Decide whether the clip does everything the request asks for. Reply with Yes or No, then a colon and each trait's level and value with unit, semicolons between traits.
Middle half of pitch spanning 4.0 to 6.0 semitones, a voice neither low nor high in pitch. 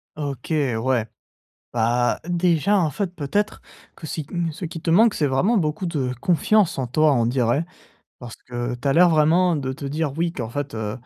Yes: average, 5.2 semitones; medium, 150 Hz